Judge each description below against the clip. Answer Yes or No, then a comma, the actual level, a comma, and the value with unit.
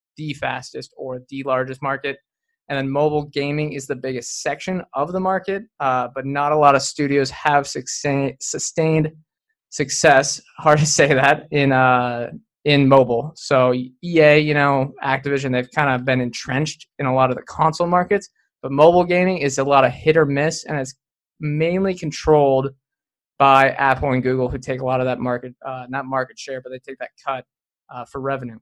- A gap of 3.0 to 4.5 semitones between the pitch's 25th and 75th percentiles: No, narrow, 2.6 semitones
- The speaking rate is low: No, average, 185 wpm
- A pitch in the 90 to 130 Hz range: No, medium, 140 Hz